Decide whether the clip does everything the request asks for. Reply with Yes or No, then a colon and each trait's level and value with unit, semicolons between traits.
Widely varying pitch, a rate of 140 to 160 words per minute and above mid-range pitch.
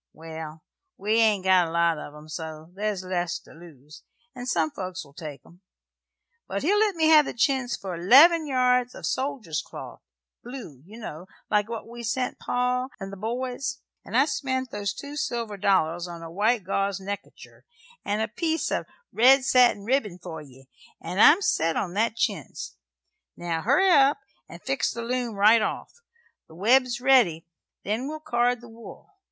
No: wide, 6.5 semitones; average, 180 wpm; high, 215 Hz